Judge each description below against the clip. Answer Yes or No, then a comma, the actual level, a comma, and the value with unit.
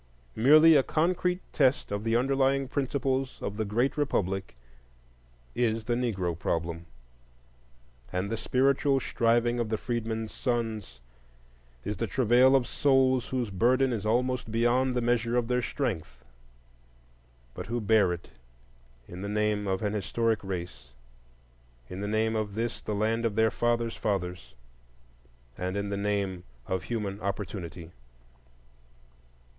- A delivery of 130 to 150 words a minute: Yes, average, 140 wpm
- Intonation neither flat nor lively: Yes, average, 3.8 semitones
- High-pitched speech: No, low, 115 Hz